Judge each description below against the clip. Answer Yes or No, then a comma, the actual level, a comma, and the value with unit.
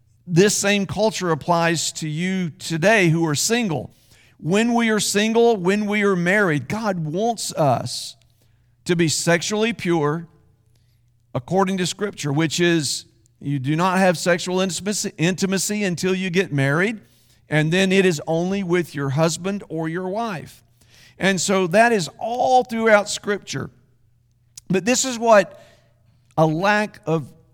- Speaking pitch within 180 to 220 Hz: No, medium, 170 Hz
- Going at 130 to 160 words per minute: Yes, average, 140 wpm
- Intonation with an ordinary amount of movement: No, wide, 6.2 semitones